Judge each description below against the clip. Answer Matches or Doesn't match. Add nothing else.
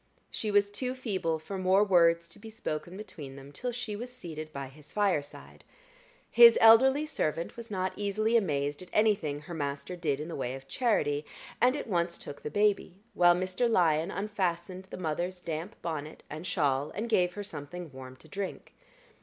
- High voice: Doesn't match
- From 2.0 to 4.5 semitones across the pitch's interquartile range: Doesn't match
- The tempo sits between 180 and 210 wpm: Matches